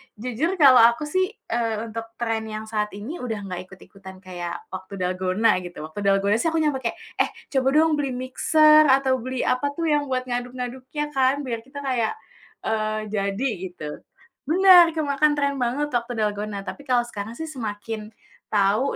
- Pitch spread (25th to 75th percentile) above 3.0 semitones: Yes, average, 5.2 semitones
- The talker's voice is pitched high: Yes, high, 240 Hz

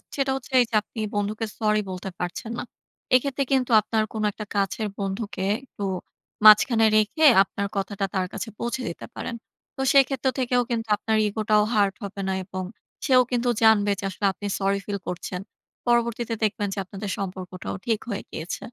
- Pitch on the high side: Yes, high, 215 Hz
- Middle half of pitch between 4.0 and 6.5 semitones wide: No, average, 3.2 semitones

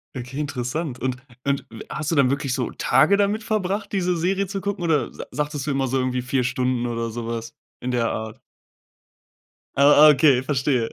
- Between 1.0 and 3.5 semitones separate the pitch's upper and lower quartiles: No, average, 4.5 semitones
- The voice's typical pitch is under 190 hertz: Yes, low, 135 Hz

